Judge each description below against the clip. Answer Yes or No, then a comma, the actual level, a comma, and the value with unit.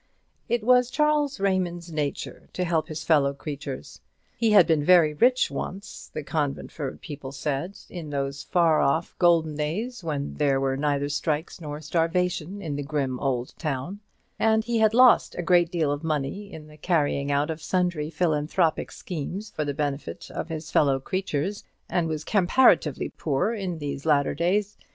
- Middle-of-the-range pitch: Yes, medium, 160 Hz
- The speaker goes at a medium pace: Yes, average, 170 wpm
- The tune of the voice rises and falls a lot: No, average, 4.2 semitones